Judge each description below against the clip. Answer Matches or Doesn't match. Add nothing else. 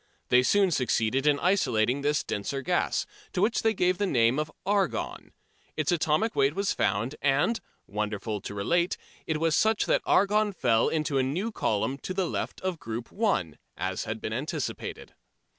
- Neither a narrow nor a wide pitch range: Doesn't match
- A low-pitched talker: Doesn't match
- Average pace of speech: Matches